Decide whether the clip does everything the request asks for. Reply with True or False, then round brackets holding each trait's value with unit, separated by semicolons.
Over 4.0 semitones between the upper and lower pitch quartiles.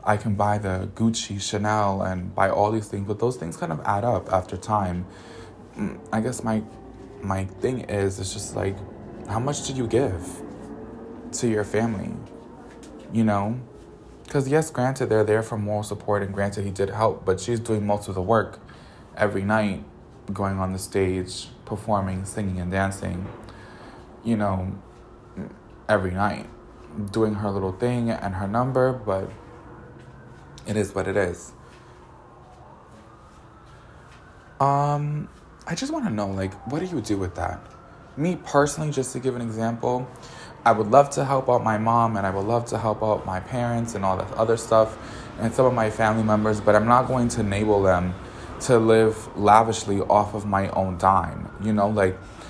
False (3.0 semitones)